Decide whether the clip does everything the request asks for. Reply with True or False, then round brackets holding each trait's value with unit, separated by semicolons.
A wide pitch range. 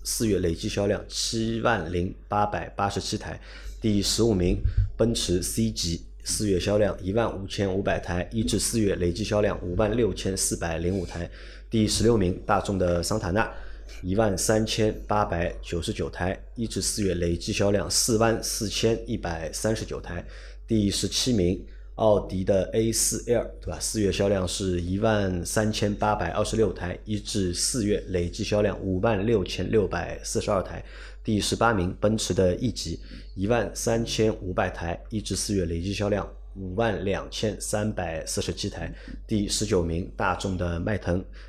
False (3.3 semitones)